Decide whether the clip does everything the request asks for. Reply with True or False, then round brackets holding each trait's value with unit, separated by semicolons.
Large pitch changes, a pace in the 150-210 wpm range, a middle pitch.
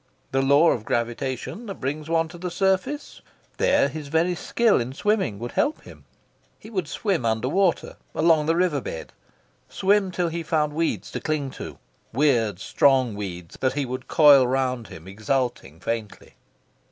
True (6.1 semitones; 165 wpm; 145 Hz)